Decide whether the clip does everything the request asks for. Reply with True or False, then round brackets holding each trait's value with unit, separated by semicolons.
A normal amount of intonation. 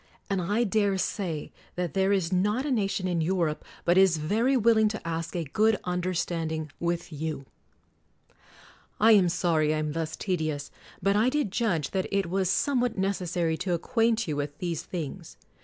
True (4.1 semitones)